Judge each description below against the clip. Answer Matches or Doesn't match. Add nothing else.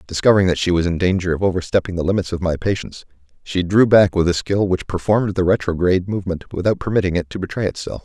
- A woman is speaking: Doesn't match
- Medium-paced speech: Doesn't match